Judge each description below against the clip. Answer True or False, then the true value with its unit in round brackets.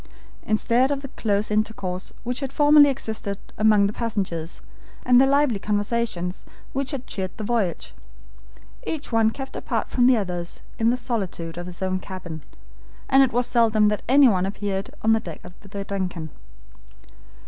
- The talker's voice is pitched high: True (215 Hz)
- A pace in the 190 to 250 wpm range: False (165 wpm)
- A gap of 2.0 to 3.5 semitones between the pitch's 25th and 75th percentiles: False (4.6 semitones)